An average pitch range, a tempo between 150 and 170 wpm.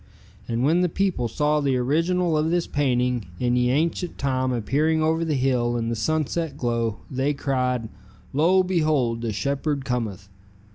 Yes: average, 4.4 semitones; average, 160 wpm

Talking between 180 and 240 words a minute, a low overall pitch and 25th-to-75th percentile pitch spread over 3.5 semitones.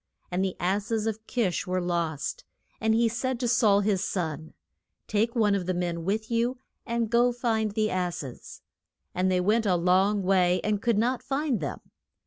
No: average, 190 wpm; high, 205 Hz; average, 4.2 semitones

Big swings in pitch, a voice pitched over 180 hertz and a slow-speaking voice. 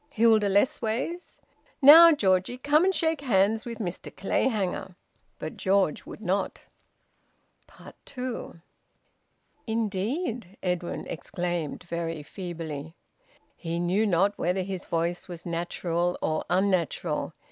No: average, 4.8 semitones; high, 190 Hz; slow, 105 wpm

